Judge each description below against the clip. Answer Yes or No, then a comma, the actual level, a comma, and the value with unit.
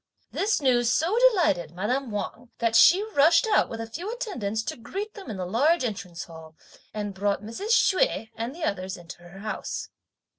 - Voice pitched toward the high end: Yes, high, 230 Hz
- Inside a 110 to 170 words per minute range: No, average, 185 wpm